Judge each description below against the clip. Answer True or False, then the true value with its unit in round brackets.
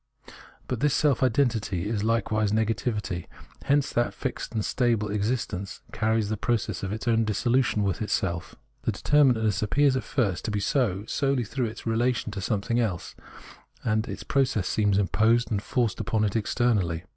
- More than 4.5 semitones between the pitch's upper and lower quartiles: False (3.0 semitones)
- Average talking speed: True (170 wpm)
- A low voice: True (110 Hz)